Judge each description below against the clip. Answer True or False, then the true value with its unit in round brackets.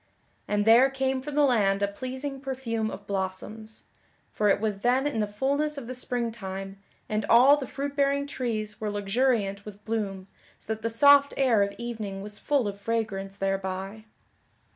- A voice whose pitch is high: True (220 Hz)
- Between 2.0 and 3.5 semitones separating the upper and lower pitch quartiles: False (4.6 semitones)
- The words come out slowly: False (180 wpm)